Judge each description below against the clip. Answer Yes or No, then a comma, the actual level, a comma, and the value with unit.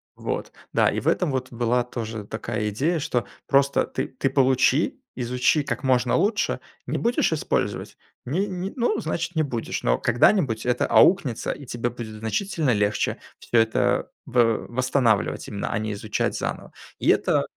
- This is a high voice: No, low, 125 Hz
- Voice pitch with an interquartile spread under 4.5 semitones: No, average, 5.1 semitones